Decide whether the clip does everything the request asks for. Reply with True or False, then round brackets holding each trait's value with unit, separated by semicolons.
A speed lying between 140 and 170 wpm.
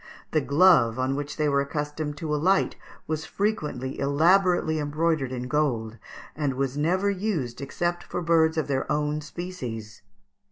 True (150 wpm)